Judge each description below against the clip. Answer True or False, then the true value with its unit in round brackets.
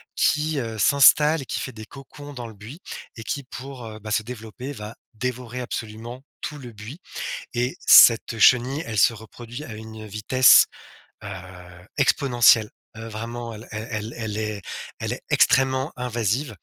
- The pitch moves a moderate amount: True (3.1 semitones)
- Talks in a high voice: False (120 Hz)